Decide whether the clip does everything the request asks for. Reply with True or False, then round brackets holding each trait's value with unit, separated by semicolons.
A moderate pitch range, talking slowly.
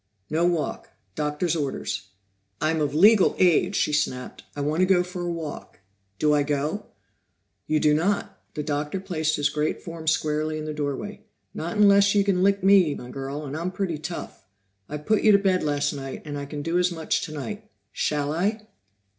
False (3.9 semitones; 190 wpm)